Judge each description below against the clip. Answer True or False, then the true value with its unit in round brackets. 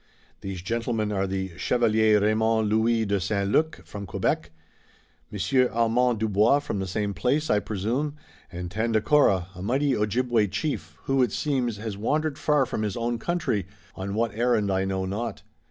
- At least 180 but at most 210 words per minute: False (165 wpm)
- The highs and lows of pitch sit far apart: False (3.6 semitones)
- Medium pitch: False (110 Hz)